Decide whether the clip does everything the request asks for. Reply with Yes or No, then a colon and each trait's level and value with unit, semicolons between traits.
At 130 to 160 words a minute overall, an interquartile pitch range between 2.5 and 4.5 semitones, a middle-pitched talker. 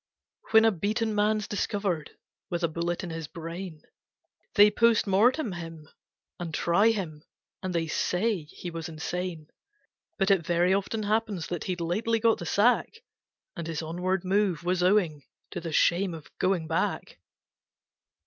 Yes: average, 155 wpm; average, 3.8 semitones; medium, 180 Hz